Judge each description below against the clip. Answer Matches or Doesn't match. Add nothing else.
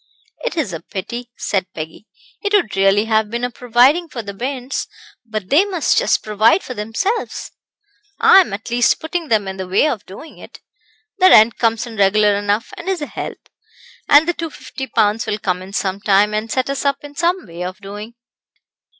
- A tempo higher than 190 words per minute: Matches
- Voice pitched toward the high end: Matches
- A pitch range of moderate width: Doesn't match